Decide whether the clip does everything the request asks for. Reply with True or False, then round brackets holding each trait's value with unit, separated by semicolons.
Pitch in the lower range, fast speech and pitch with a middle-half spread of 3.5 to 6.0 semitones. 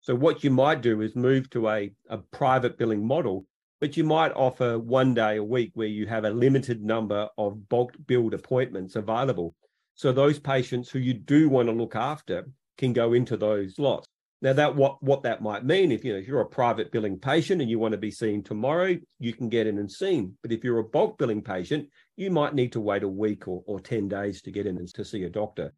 True (120 Hz; 235 wpm; 3.8 semitones)